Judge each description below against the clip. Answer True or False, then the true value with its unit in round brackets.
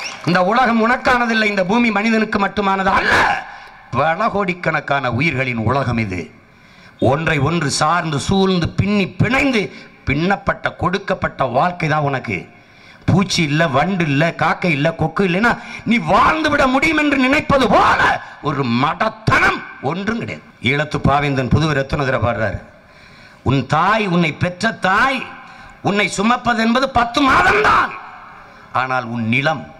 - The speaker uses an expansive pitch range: True (7.8 semitones)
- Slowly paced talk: True (125 wpm)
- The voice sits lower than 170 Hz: False (175 Hz)